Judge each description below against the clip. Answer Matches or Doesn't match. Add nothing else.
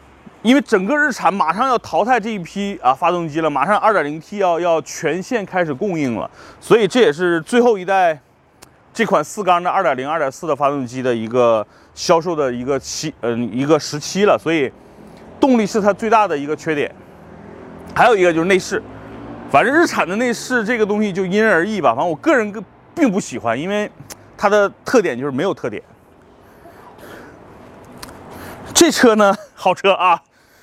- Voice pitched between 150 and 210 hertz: Matches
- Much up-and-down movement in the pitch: Matches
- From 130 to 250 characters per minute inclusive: Doesn't match